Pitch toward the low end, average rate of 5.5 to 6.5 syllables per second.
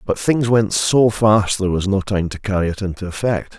No: low, 100 Hz; 5.2 syllables/s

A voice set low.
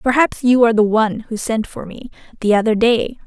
No: high, 225 Hz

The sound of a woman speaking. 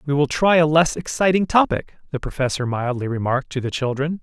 No: male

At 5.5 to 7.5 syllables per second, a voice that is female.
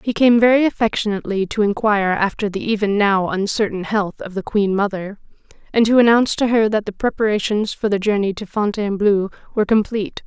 Yes: 6.0 syllables/s; female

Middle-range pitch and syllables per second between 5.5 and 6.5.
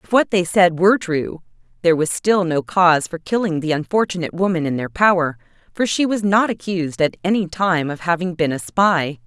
Yes: medium, 175 Hz; 5.6 syllables/s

